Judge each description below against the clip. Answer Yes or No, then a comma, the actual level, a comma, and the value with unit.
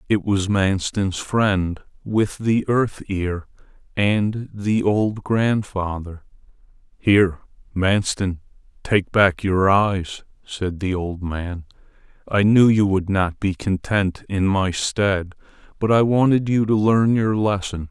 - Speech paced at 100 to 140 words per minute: Yes, slow, 135 wpm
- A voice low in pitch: Yes, low, 100 Hz